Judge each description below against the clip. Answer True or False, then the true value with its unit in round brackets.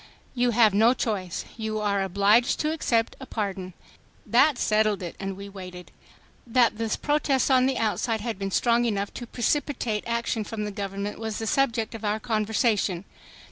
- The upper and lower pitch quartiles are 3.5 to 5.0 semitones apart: False (3.0 semitones)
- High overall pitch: True (220 Hz)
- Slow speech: False (175 wpm)